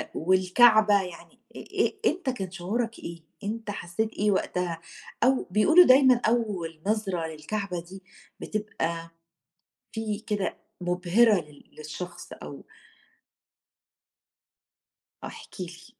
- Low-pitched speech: No, high, 200 Hz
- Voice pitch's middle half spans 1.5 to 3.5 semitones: No, average, 4.2 semitones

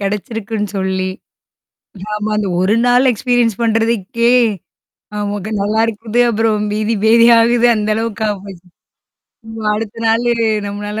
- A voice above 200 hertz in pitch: Yes, high, 220 Hz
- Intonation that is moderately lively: No, narrow, 1.8 semitones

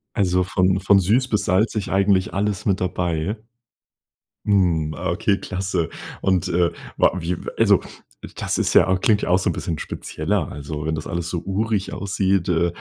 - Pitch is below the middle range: Yes, very low, 95 Hz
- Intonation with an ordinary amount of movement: No, narrow, 2.3 semitones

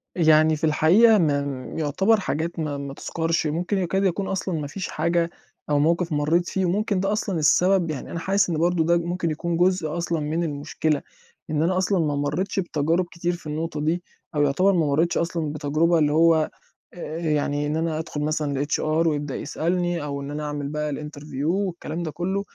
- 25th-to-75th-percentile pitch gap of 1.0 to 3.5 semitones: Yes, average, 2.8 semitones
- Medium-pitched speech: Yes, medium, 160 Hz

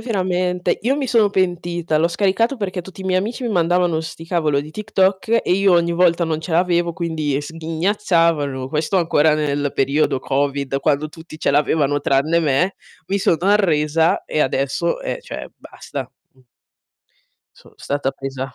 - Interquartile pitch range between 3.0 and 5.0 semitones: Yes, average, 3.9 semitones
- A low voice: No, medium, 165 Hz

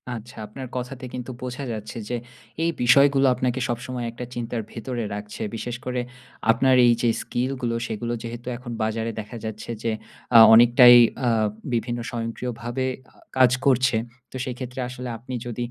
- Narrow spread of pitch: Yes, narrow, 1.6 semitones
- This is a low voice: Yes, low, 120 Hz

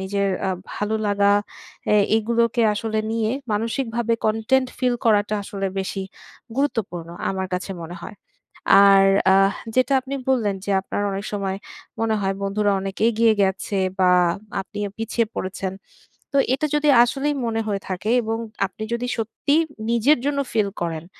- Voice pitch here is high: Yes, high, 215 Hz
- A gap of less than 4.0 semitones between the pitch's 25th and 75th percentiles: Yes, average, 3.1 semitones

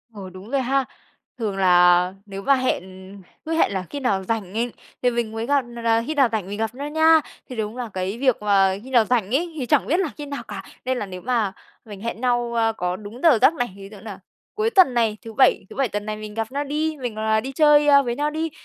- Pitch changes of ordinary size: Yes, average, 5.0 semitones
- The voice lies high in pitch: Yes, high, 235 Hz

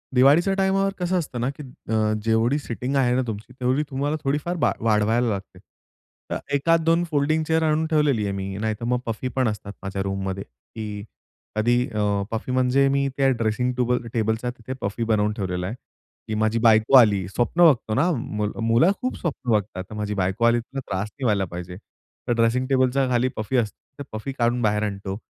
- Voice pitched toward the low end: Yes, low, 120 Hz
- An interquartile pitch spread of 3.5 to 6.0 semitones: Yes, average, 4.4 semitones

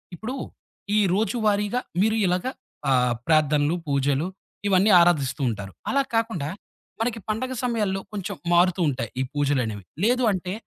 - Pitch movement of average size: No, wide, 7.3 semitones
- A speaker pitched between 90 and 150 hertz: No, medium, 180 Hz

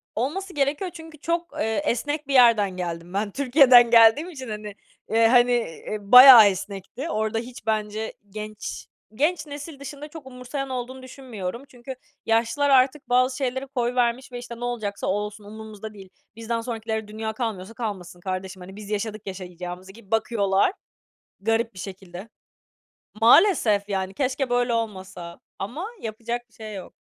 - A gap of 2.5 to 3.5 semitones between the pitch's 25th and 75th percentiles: No, average, 4.1 semitones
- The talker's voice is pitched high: Yes, high, 230 Hz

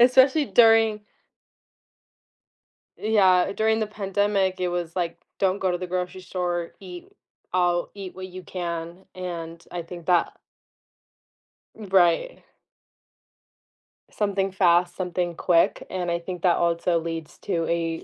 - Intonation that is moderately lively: No, narrow, 2.2 semitones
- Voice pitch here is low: No, medium, 180 Hz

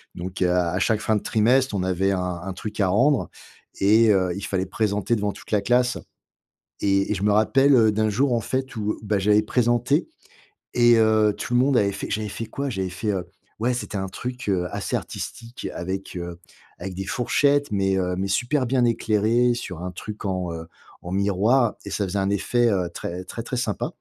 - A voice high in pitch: No, low, 105 Hz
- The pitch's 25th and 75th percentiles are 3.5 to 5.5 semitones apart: Yes, average, 4.0 semitones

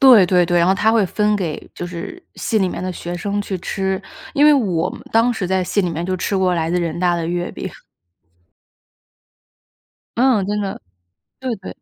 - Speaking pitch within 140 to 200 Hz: Yes, high, 190 Hz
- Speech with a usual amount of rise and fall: Yes, average, 3.2 semitones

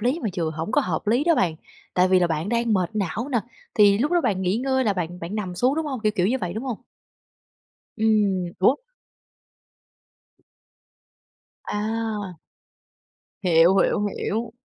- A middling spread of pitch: Yes, average, 4.6 semitones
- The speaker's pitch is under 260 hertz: Yes, high, 210 Hz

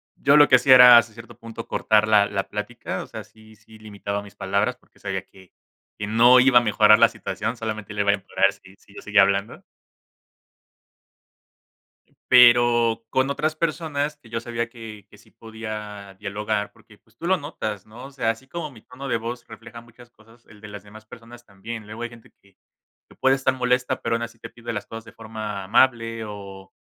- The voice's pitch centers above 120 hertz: No, low, 115 Hz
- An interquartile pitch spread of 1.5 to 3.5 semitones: Yes, narrow, 2.6 semitones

